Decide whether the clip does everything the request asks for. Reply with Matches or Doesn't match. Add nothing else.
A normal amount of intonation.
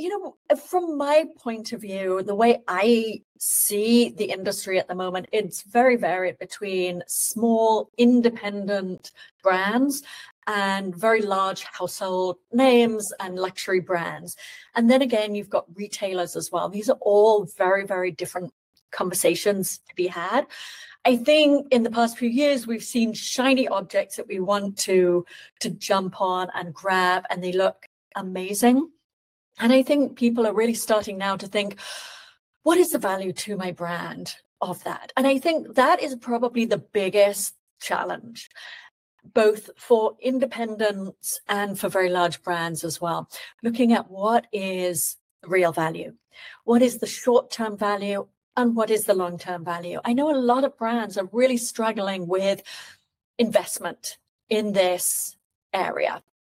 Matches